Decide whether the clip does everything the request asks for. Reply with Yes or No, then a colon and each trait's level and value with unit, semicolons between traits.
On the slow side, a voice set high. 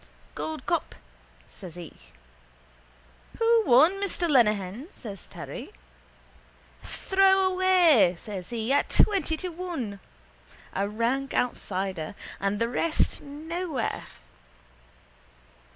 Yes: slow, 90 wpm; very high, 270 Hz